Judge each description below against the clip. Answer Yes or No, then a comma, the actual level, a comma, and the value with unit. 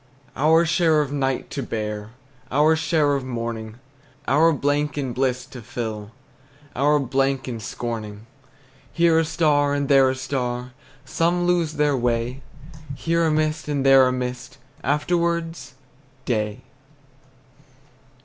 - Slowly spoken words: Yes, slow, 130 wpm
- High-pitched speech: No, low, 135 Hz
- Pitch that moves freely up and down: No, average, 3.9 semitones